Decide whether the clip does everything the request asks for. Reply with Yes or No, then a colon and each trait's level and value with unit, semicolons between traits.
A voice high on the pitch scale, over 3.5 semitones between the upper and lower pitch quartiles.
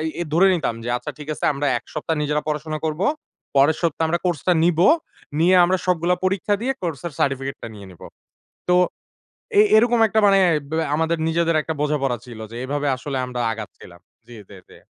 No: medium, 155 Hz; average, 4.1 semitones